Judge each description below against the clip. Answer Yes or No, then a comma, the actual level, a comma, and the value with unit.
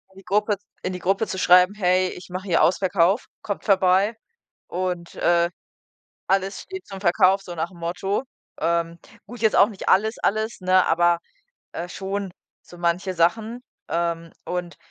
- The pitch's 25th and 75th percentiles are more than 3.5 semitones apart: No, narrow, 2.4 semitones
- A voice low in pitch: No, medium, 185 Hz